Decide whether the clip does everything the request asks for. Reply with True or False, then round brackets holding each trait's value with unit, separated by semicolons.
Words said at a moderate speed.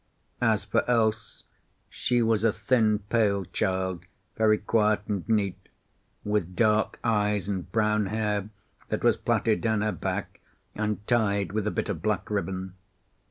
True (150 wpm)